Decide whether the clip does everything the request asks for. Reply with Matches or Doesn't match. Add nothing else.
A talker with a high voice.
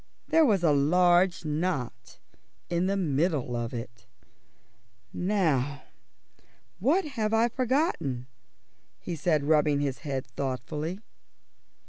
Doesn't match